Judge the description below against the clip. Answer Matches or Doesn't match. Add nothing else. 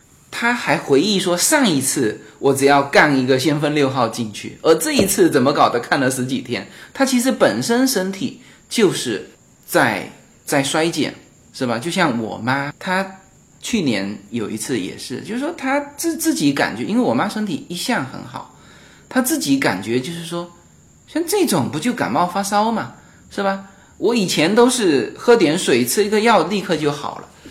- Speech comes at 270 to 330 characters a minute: Doesn't match